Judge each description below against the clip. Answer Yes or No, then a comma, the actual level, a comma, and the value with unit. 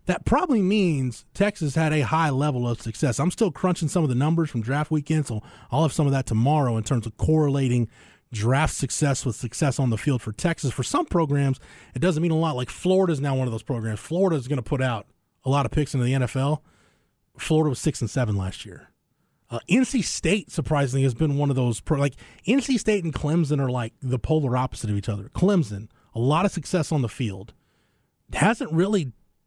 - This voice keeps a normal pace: No, fast, 225 wpm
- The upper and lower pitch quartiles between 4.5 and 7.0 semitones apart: Yes, average, 4.8 semitones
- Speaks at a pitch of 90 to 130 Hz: No, medium, 140 Hz